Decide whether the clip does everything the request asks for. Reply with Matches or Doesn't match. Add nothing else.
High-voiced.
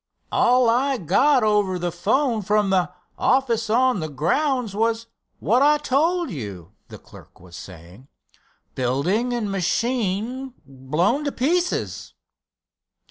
Matches